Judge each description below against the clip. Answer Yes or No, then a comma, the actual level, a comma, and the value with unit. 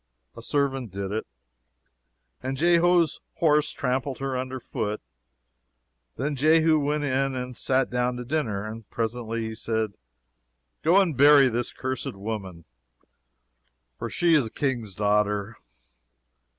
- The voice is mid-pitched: No, low, 125 Hz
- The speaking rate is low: Yes, slow, 130 wpm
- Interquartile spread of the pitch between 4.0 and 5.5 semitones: Yes, average, 4.6 semitones